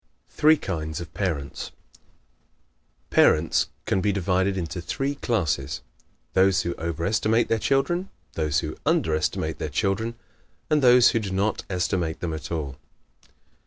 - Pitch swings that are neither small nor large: No, wide, 5.7 semitones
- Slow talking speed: No, average, 145 wpm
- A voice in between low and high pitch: No, very low, 95 Hz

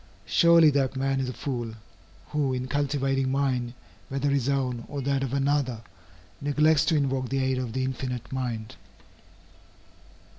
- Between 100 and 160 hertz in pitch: Yes, low, 135 Hz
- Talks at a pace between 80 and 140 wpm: No, average, 150 wpm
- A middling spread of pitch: No, narrow, 1.6 semitones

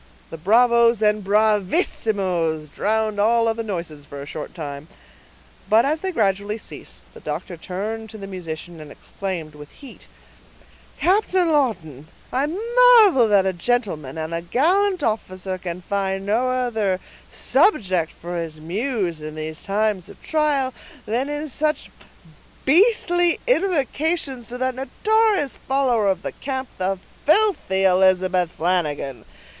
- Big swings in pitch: Yes, wide, 7.2 semitones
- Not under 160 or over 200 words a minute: No, slow, 135 wpm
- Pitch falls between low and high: No, high, 210 Hz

